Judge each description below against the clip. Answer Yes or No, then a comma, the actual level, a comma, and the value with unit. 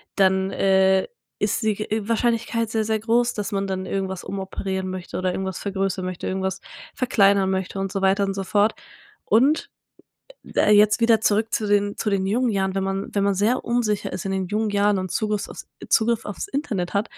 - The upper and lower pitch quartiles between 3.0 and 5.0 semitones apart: No, narrow, 2.4 semitones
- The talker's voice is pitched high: Yes, high, 200 Hz